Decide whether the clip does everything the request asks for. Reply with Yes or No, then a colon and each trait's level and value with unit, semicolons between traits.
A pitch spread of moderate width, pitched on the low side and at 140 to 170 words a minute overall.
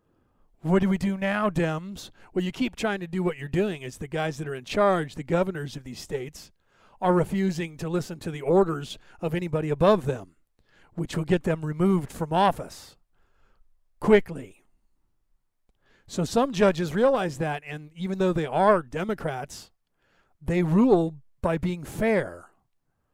No: average, 3.8 semitones; medium, 175 Hz; average, 160 wpm